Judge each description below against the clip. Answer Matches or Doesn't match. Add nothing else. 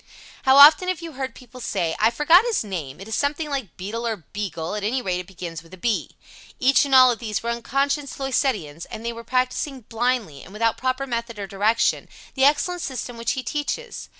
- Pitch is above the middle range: Matches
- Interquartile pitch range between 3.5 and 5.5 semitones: Matches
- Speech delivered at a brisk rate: Matches